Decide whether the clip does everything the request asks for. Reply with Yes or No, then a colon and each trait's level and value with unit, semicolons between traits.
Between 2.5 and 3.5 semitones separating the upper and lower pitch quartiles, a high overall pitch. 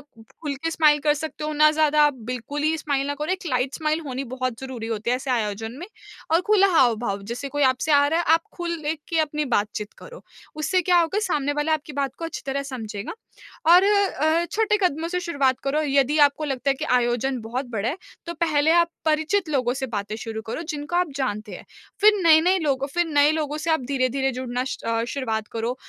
No: average, 3.9 semitones; very high, 285 Hz